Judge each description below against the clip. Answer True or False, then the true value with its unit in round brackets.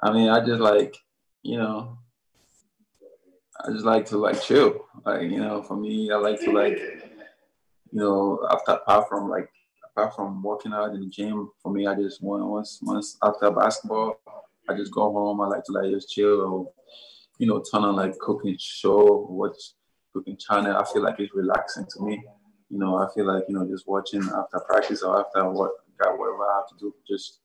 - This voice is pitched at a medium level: False (105 Hz)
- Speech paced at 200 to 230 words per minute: True (205 wpm)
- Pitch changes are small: True (1.8 semitones)